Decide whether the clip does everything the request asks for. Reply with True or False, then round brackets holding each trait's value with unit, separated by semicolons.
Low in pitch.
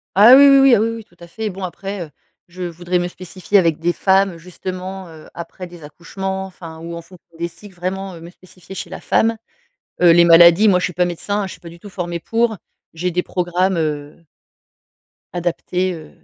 False (180 Hz)